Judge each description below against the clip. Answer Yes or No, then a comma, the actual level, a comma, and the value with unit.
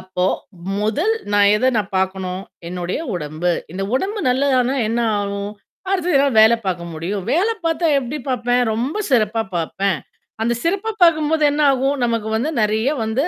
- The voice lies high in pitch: Yes, high, 230 Hz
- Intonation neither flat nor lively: No, wide, 6.4 semitones